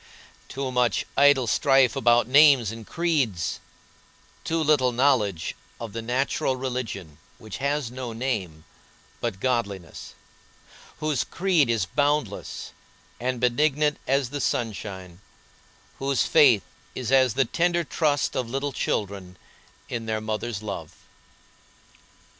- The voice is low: Yes, low, 125 Hz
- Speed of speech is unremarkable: No, slow, 120 wpm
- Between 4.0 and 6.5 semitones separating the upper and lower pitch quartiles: Yes, average, 4.4 semitones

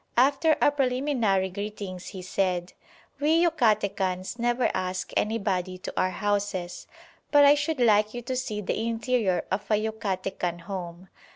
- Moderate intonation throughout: Yes, average, 5.0 semitones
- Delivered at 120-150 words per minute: Yes, average, 145 wpm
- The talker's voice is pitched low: No, high, 210 Hz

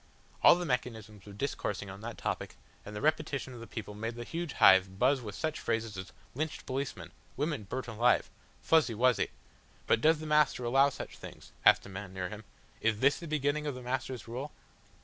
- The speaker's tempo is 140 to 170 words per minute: No, average, 200 wpm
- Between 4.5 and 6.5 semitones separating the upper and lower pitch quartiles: Yes, average, 5.2 semitones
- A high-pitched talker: No, low, 125 Hz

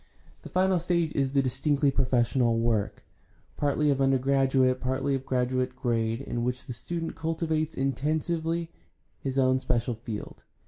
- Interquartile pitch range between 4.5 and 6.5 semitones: No, average, 3.6 semitones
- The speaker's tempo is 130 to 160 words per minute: Yes, average, 140 wpm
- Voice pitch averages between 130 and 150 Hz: Yes, low, 135 Hz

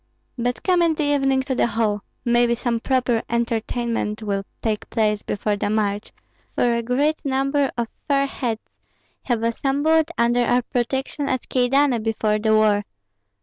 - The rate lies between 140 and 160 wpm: Yes, average, 155 wpm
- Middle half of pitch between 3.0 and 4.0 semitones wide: Yes, average, 3.4 semitones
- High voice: Yes, high, 240 Hz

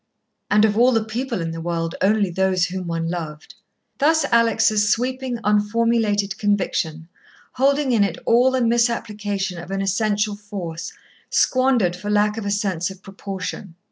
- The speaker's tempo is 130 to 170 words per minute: Yes, average, 155 wpm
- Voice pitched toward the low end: No, high, 205 Hz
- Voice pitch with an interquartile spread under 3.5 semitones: No, average, 3.9 semitones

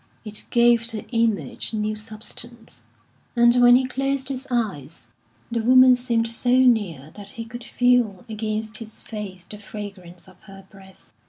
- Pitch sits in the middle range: No, high, 225 Hz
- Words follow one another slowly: No, average, 155 wpm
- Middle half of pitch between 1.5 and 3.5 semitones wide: Yes, average, 3.0 semitones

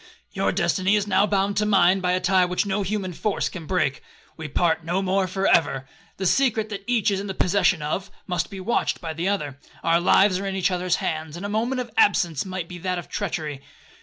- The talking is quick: Yes, fast, 225 wpm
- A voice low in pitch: No, medium, 185 Hz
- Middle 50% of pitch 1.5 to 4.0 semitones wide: Yes, average, 2.7 semitones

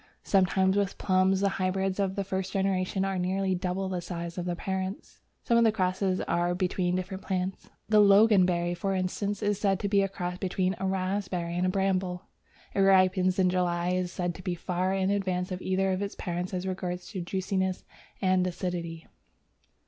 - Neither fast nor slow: Yes, average, 190 wpm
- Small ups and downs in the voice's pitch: Yes, narrow, 1.2 semitones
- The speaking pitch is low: No, medium, 185 Hz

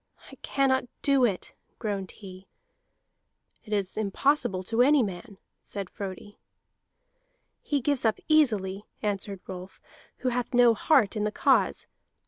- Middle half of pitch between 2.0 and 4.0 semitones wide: No, average, 4.6 semitones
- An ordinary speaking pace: No, slow, 130 wpm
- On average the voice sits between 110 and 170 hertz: No, high, 215 Hz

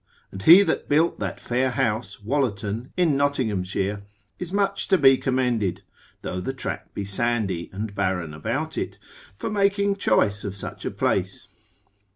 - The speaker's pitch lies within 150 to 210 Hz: No, low, 120 Hz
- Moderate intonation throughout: No, wide, 6.5 semitones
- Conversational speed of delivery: Yes, average, 155 wpm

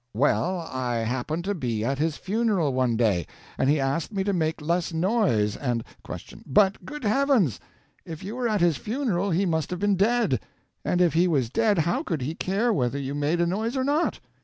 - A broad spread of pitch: Yes, wide, 6.9 semitones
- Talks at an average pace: No, fast, 210 wpm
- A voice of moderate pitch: Yes, medium, 170 Hz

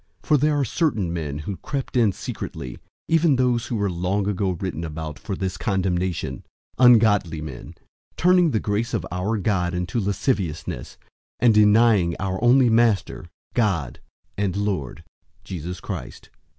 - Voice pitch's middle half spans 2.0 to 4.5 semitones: No, average, 4.9 semitones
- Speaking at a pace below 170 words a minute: Yes, average, 150 wpm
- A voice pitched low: Yes, low, 100 Hz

